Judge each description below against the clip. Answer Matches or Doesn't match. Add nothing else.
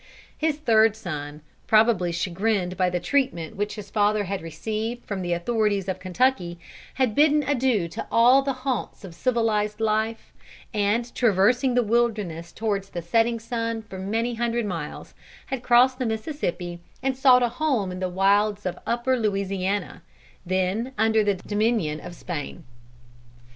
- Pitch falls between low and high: Doesn't match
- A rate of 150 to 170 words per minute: Matches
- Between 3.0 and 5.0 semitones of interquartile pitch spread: Matches